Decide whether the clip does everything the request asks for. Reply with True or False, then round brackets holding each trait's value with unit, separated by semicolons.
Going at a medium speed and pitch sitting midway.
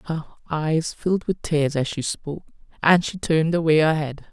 True (195 wpm; 155 Hz)